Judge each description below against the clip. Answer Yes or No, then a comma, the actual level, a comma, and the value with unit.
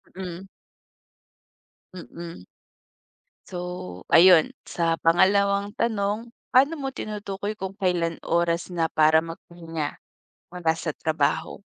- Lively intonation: No, average, 3.3 semitones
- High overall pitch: No, medium, 175 Hz